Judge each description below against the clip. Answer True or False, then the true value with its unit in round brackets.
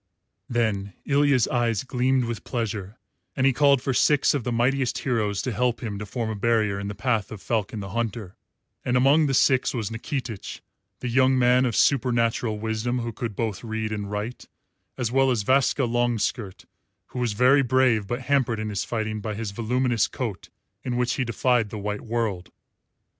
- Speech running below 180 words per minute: False (185 wpm)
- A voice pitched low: True (120 Hz)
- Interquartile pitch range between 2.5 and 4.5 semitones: True (2.9 semitones)